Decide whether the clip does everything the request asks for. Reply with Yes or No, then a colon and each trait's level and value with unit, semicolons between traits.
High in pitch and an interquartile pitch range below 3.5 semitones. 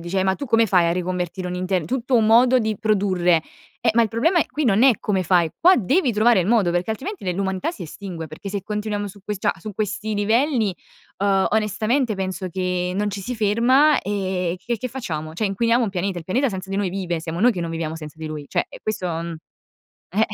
No: high, 200 Hz; average, 4.0 semitones